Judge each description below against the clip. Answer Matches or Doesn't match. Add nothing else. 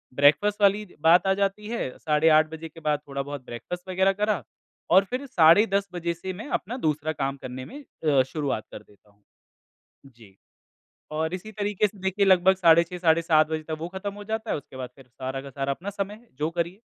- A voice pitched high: Doesn't match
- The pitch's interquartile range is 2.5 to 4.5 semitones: Doesn't match